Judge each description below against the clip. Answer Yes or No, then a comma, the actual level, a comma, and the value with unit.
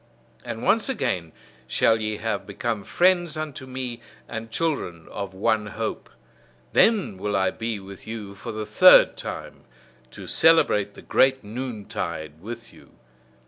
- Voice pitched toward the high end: No, low, 110 Hz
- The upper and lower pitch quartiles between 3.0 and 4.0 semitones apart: No, average, 4.7 semitones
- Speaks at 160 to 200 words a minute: No, average, 145 wpm